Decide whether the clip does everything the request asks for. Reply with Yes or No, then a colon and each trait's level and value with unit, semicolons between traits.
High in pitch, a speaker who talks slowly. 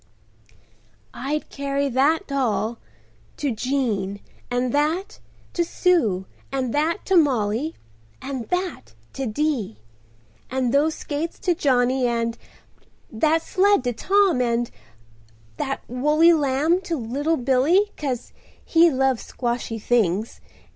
Yes: very high, 265 Hz; slow, 100 wpm